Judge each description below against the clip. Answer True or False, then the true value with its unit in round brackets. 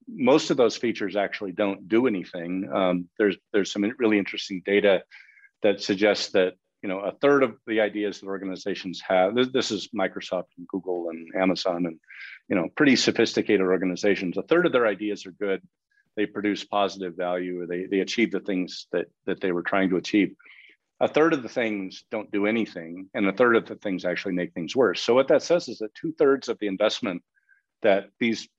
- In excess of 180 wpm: True (200 wpm)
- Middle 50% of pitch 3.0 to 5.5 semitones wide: True (3.3 semitones)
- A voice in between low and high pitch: False (100 Hz)